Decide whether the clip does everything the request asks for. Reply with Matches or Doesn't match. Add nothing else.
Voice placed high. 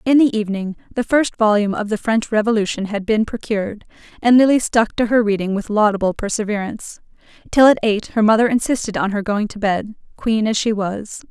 Matches